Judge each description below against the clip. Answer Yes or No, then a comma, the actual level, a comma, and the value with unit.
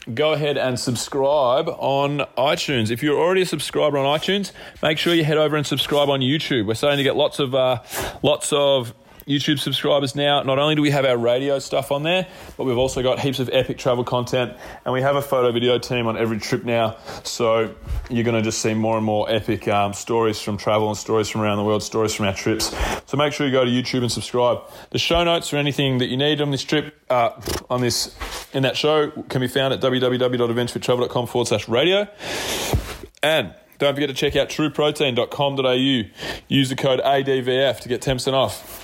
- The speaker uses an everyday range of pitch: Yes, average, 3.2 semitones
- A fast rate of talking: Yes, fast, 210 wpm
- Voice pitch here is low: Yes, low, 130 Hz